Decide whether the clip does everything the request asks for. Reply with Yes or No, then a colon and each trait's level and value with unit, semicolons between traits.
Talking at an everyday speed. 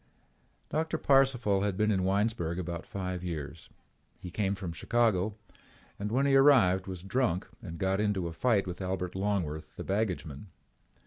Yes: average, 155 wpm